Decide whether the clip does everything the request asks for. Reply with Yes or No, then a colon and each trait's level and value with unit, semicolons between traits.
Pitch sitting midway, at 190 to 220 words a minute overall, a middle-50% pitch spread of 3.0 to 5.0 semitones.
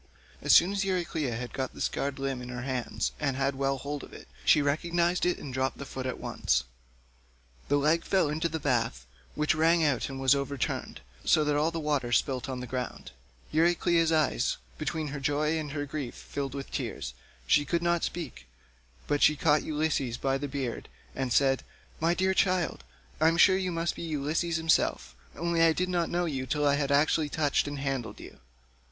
Yes: medium, 145 Hz; fast, 205 wpm; average, 3.6 semitones